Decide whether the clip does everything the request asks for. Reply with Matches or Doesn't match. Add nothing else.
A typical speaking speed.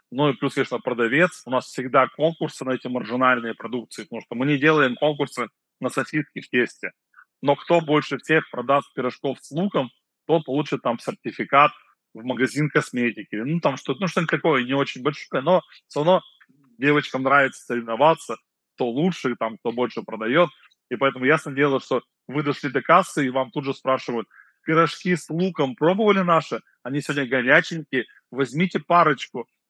Doesn't match